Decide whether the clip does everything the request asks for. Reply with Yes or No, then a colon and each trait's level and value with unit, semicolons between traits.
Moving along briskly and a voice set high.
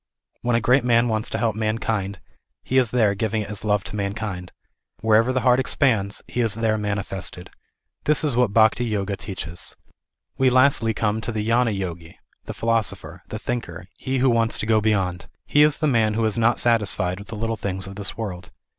No: fast, 210 wpm; low, 110 Hz